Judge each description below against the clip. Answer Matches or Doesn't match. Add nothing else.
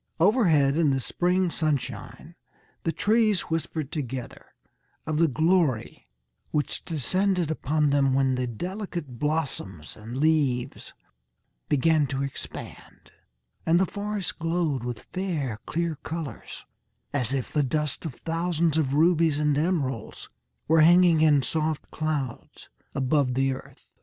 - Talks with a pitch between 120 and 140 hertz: Doesn't match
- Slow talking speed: Matches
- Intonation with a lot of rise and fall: Doesn't match